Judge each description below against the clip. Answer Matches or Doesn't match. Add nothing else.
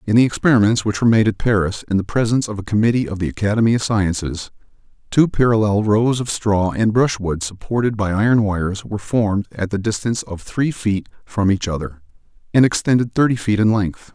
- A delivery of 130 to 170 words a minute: Doesn't match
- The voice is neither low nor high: Doesn't match